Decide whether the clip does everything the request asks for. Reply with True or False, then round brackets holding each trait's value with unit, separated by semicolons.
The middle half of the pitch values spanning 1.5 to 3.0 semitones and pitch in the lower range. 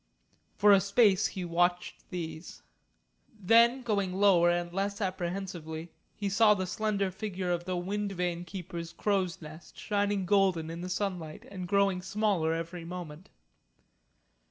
False (2.6 semitones; 185 Hz)